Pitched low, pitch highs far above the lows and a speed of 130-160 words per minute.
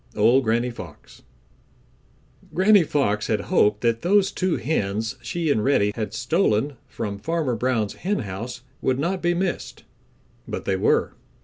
Yes: low, 125 Hz; wide, 8.0 semitones; average, 140 wpm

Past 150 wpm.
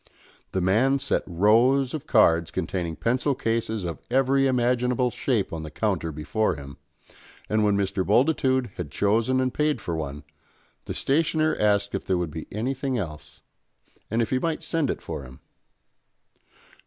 Yes: average, 160 wpm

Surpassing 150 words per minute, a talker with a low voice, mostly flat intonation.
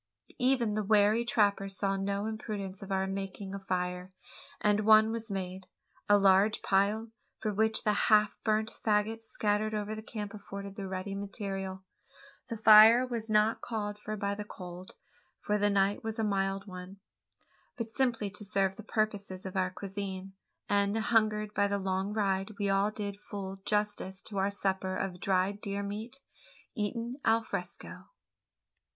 No: average, 160 wpm; high, 205 Hz; narrow, 1.8 semitones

